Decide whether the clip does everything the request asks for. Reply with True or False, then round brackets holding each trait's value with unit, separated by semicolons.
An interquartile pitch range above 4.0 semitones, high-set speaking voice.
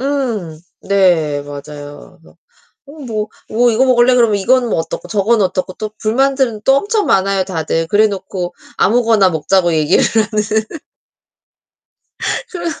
True (5.6 semitones; 210 Hz)